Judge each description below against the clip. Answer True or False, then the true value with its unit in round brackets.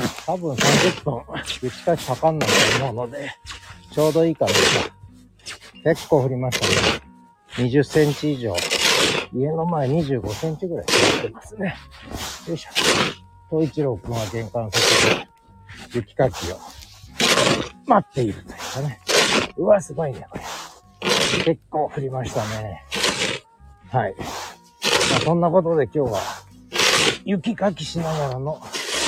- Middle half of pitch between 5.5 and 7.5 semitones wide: True (7.0 semitones)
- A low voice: True (130 Hz)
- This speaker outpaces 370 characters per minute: False (245 characters per minute)